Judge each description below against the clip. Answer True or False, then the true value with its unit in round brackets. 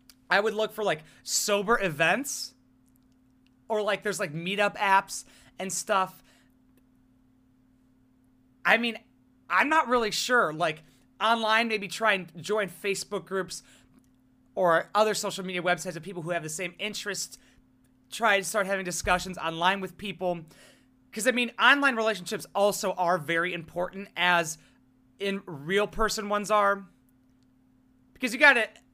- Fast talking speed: False (140 wpm)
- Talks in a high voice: False (180 Hz)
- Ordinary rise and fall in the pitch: False (8.1 semitones)